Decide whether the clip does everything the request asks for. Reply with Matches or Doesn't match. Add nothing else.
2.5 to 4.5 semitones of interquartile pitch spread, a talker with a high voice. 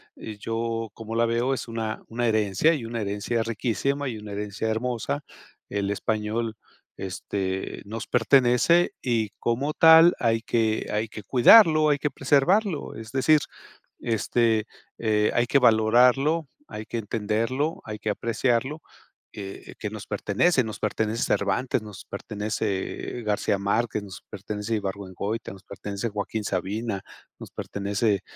Doesn't match